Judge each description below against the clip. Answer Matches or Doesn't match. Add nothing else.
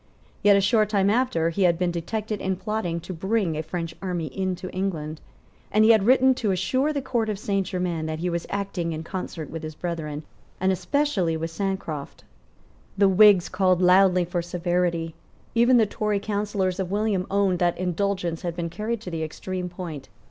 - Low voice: Doesn't match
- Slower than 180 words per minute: Doesn't match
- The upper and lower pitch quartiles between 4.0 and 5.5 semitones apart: Doesn't match